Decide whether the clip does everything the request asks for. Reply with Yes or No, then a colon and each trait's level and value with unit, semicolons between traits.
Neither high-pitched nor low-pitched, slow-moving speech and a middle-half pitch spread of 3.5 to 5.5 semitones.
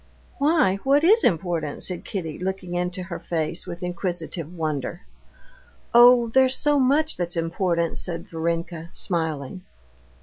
Yes: medium, 175 Hz; slow, 130 wpm; average, 5.1 semitones